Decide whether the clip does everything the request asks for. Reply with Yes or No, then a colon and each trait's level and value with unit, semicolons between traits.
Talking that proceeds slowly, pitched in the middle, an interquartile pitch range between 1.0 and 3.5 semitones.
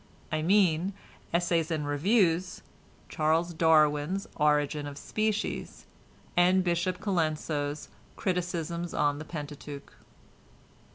Yes: slow, 95 wpm; medium, 165 Hz; average, 3.2 semitones